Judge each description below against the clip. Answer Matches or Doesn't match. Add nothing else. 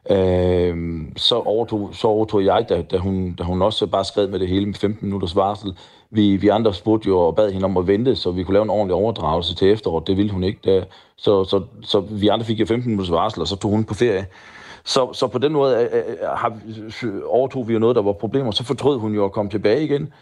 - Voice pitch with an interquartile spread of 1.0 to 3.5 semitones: Matches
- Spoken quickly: Matches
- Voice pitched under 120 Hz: Matches